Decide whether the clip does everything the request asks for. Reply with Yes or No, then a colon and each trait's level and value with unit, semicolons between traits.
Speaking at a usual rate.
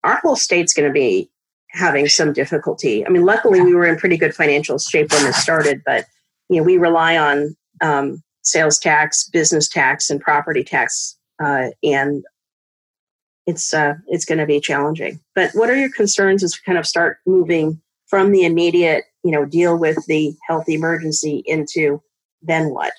Yes: average, 180 wpm